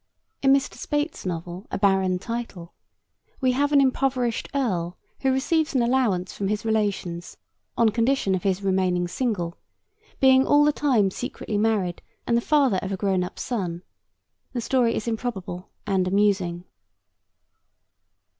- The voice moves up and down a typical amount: No, wide, 5.7 semitones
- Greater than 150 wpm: No, average, 145 wpm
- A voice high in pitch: Yes, high, 210 Hz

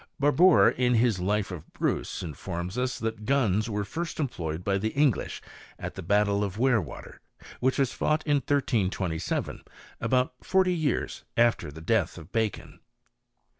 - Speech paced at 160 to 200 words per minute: No, average, 150 wpm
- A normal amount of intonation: No, wide, 5.8 semitones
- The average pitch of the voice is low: Yes, low, 110 Hz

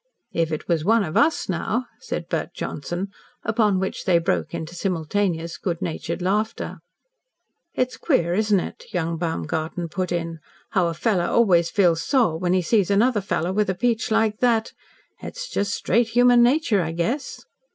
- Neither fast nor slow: Yes, average, 170 wpm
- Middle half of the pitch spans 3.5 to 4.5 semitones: No, average, 4.9 semitones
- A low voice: No, high, 190 Hz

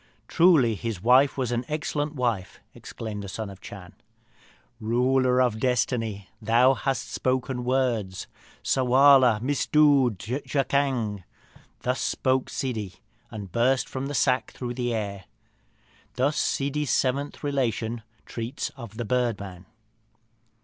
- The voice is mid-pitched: No, low, 125 Hz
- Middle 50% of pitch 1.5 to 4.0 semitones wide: Yes, average, 3.4 semitones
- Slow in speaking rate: Yes, slow, 125 wpm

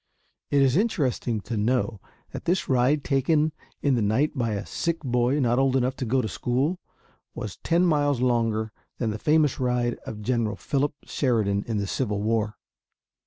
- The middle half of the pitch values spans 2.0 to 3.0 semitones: No, average, 4.3 semitones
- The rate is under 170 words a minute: No, average, 175 wpm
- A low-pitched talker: Yes, low, 125 Hz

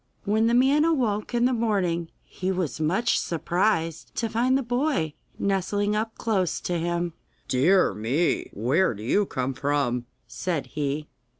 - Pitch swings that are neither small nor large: No, wide, 6.4 semitones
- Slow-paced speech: No, average, 155 wpm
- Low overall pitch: No, medium, 185 Hz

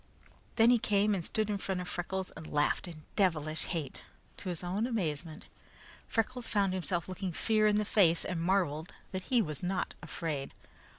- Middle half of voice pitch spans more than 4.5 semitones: No, average, 4.0 semitones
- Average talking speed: Yes, average, 180 wpm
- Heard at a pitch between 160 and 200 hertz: Yes, medium, 185 Hz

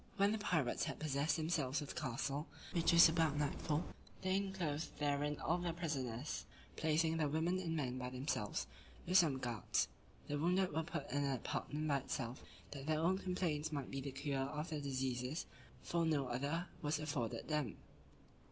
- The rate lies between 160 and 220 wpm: Yes, average, 180 wpm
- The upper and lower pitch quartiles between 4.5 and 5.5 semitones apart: No, average, 3.2 semitones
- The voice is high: No, medium, 150 Hz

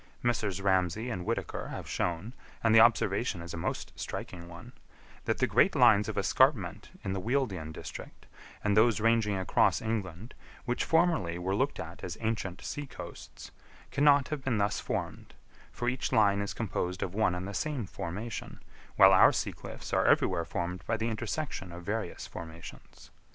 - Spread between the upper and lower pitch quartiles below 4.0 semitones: No, average, 4.6 semitones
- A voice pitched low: Yes, low, 105 Hz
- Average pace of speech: Yes, average, 170 wpm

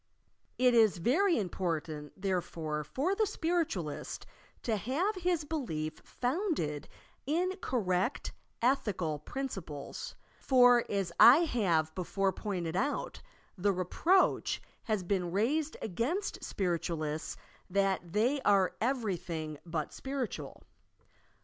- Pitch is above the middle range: Yes, high, 205 Hz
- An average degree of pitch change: No, wide, 7.9 semitones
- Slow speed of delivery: Yes, slow, 105 wpm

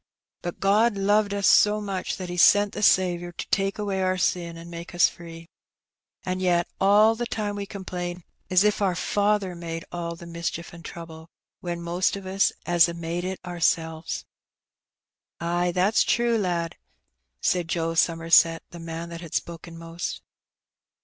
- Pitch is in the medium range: Yes, medium, 175 Hz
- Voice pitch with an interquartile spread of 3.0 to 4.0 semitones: No, narrow, 2.6 semitones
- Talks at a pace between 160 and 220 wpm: Yes, average, 170 wpm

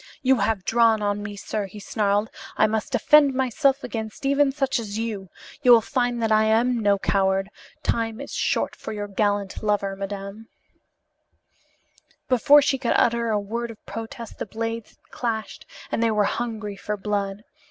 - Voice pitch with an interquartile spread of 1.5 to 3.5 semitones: Yes, narrow, 2.5 semitones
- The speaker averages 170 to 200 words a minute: Yes, average, 175 wpm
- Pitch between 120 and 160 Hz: No, high, 220 Hz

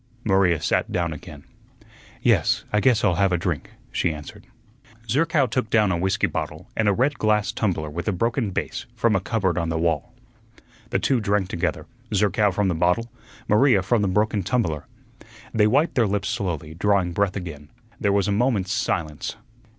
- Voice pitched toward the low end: Yes, low, 100 Hz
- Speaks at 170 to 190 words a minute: Yes, average, 180 wpm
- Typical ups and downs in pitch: Yes, average, 3.9 semitones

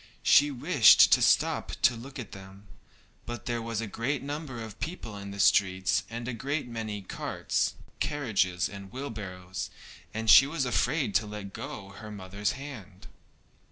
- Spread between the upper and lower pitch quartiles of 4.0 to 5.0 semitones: Yes, average, 4.5 semitones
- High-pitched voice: No, low, 110 Hz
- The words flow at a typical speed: Yes, average, 160 wpm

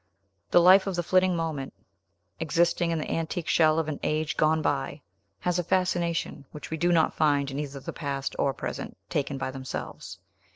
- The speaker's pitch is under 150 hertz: No, medium, 160 Hz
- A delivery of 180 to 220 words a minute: Yes, average, 190 wpm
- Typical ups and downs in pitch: Yes, average, 3.3 semitones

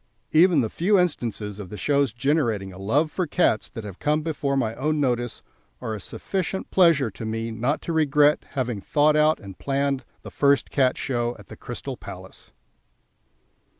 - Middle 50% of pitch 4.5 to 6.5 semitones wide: Yes, average, 5.3 semitones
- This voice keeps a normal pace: Yes, average, 180 wpm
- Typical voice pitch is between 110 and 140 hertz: Yes, low, 135 Hz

